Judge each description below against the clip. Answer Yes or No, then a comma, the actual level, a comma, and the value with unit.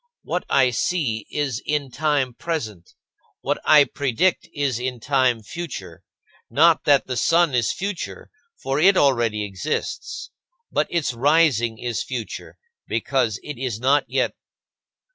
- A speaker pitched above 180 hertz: No, low, 135 Hz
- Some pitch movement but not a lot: Yes, average, 4.4 semitones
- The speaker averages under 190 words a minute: Yes, slow, 135 wpm